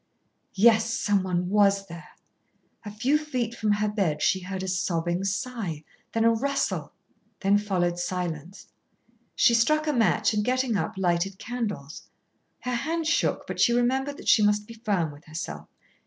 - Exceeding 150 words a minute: Yes, average, 160 wpm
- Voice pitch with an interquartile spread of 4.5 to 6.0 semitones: Yes, average, 4.8 semitones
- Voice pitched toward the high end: Yes, high, 205 Hz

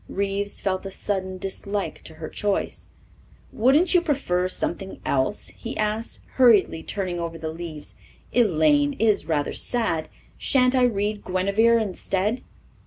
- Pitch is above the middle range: Yes, high, 195 Hz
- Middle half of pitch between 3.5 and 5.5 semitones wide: Yes, average, 4.6 semitones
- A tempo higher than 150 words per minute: No, slow, 135 wpm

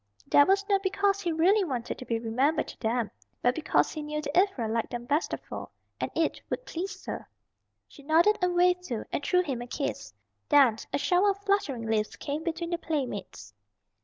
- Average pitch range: No, wide, 6.7 semitones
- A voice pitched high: Yes, very high, 315 Hz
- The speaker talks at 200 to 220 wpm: Yes, fast, 205 wpm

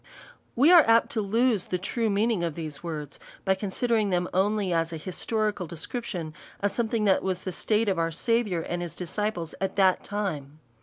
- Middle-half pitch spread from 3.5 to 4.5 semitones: Yes, average, 4.2 semitones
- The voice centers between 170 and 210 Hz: Yes, high, 190 Hz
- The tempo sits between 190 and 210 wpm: Yes, average, 200 wpm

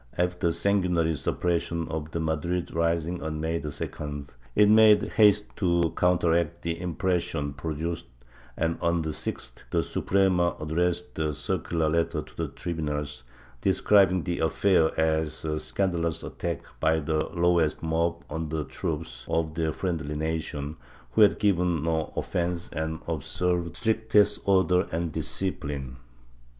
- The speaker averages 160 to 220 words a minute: No, average, 140 wpm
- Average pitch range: No, narrow, 2.1 semitones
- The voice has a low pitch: Yes, very low, 85 Hz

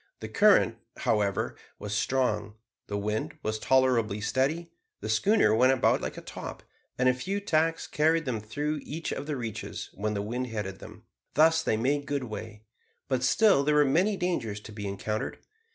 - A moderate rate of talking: Yes, average, 180 wpm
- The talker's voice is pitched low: Yes, low, 130 Hz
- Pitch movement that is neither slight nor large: No, wide, 6.0 semitones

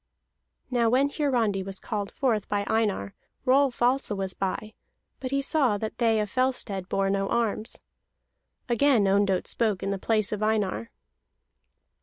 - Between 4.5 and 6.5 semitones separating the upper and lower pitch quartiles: No, average, 4.0 semitones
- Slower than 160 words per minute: Yes, average, 150 wpm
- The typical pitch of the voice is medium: No, high, 215 Hz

